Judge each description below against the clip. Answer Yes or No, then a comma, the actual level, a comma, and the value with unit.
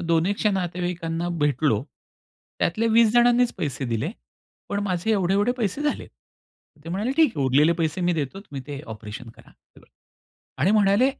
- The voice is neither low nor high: Yes, medium, 180 Hz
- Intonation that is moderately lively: No, wide, 6.3 semitones